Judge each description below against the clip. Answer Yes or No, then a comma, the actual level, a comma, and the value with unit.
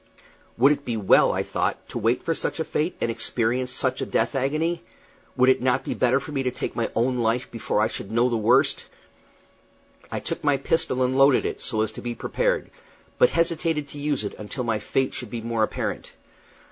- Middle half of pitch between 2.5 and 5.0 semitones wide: Yes, average, 3.6 semitones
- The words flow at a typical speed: No, fast, 215 wpm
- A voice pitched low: Yes, low, 130 Hz